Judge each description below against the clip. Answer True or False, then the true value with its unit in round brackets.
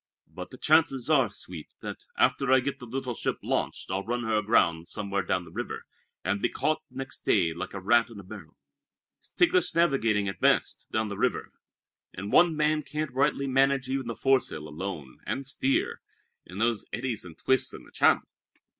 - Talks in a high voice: False (120 Hz)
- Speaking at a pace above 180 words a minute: True (190 wpm)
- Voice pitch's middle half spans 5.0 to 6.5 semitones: True (5.5 semitones)